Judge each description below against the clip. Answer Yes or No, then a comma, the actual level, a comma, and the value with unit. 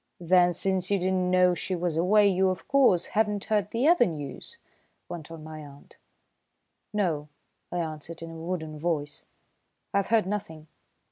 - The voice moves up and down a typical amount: Yes, average, 3.6 semitones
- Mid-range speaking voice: Yes, medium, 180 Hz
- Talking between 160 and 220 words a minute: Yes, average, 175 wpm